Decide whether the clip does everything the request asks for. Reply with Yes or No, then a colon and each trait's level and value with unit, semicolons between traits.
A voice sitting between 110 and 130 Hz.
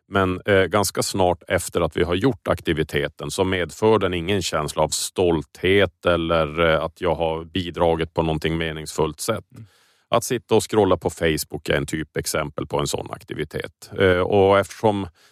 No: very low, 85 Hz